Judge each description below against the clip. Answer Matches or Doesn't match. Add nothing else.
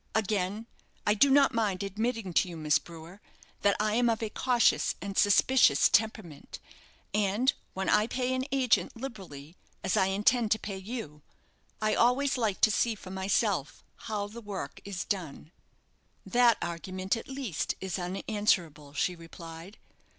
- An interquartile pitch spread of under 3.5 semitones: Doesn't match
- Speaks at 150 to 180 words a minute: Matches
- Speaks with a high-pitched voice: Matches